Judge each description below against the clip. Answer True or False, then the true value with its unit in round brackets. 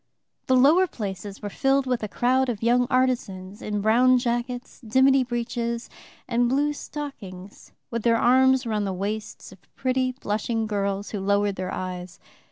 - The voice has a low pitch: False (235 Hz)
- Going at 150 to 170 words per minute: True (160 wpm)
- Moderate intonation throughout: True (3.9 semitones)